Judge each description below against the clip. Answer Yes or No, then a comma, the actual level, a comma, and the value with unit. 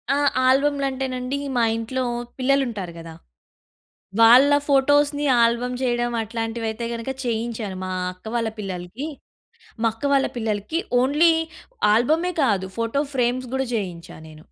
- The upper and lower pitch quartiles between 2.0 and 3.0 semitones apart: No, average, 3.4 semitones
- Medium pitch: No, high, 240 Hz